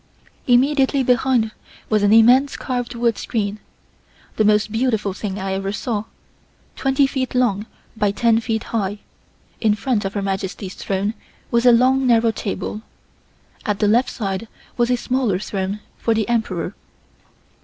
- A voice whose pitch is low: No, high, 225 Hz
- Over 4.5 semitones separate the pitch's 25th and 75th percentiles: No, average, 3.3 semitones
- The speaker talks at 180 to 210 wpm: No, average, 150 wpm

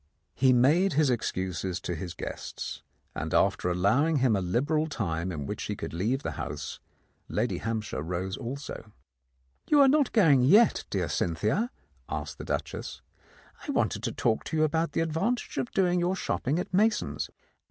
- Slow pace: No, average, 175 wpm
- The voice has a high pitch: No, low, 130 Hz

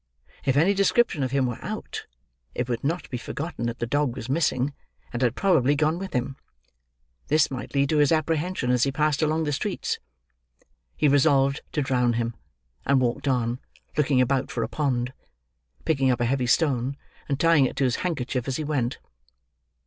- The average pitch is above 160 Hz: No, low, 135 Hz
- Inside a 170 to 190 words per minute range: Yes, average, 185 wpm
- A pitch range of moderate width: Yes, average, 3.4 semitones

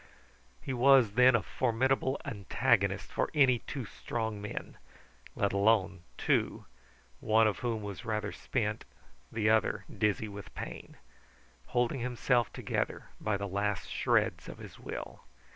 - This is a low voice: Yes, low, 110 Hz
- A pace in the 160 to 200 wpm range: No, slow, 135 wpm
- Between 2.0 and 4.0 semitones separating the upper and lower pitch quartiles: Yes, average, 3.1 semitones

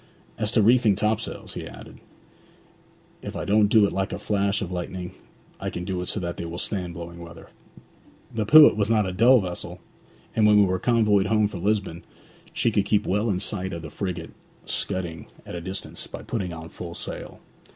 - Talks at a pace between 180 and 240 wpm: Yes, fast, 205 wpm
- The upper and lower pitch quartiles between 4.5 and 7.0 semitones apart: No, average, 3.3 semitones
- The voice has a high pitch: No, low, 100 Hz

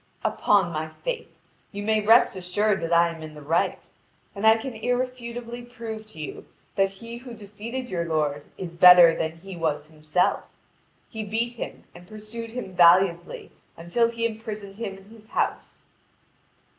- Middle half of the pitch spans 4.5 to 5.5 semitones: Yes, average, 5.2 semitones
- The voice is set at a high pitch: Yes, high, 205 Hz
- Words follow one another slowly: No, average, 165 wpm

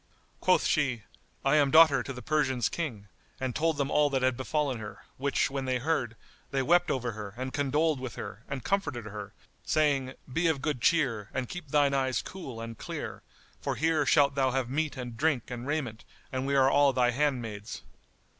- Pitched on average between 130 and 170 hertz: Yes, low, 135 Hz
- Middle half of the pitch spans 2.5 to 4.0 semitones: Yes, average, 3.3 semitones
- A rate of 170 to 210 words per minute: Yes, average, 195 wpm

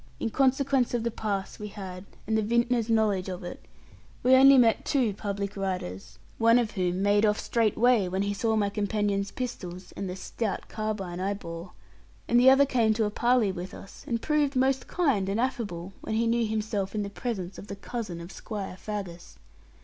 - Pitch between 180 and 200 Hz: No, high, 210 Hz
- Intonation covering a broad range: No, average, 3.5 semitones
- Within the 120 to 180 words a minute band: No, average, 195 wpm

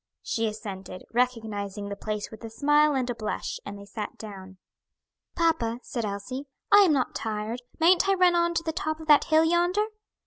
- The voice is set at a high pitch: Yes, high, 245 Hz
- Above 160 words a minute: Yes, average, 195 wpm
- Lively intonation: Yes, wide, 7.3 semitones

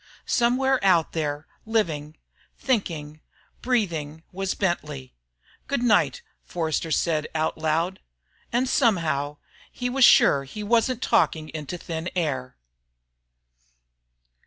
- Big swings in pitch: Yes, wide, 6.9 semitones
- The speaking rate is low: Yes, slow, 105 wpm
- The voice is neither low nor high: Yes, medium, 170 Hz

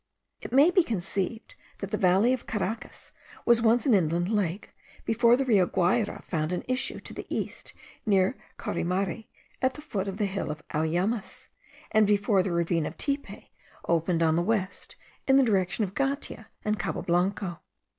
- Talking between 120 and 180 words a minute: Yes, average, 175 wpm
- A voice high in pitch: Yes, high, 200 Hz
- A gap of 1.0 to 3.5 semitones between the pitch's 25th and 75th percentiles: No, average, 4.6 semitones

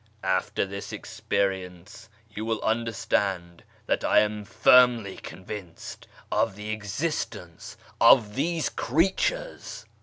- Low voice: Yes, low, 105 Hz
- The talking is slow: Yes, slow, 110 wpm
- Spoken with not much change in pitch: No, average, 3.6 semitones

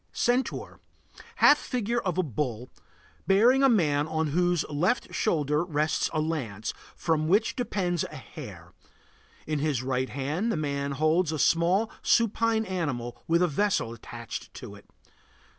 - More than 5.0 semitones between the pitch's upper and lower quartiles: Yes, wide, 5.4 semitones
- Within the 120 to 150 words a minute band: Yes, average, 145 wpm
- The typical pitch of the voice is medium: Yes, medium, 160 Hz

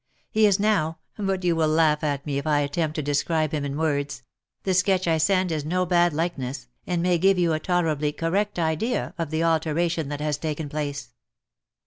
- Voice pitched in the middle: Yes, medium, 160 Hz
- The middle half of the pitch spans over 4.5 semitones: No, average, 3.1 semitones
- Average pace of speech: No, fast, 215 wpm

